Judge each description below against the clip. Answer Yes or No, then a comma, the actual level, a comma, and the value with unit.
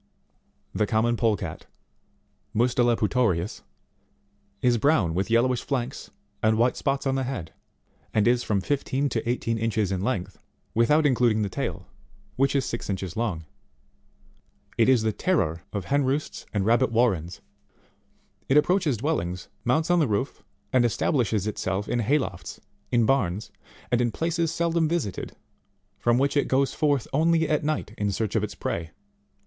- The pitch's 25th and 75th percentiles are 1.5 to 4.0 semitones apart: No, average, 4.9 semitones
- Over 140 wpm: Yes, average, 160 wpm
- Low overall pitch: Yes, low, 120 Hz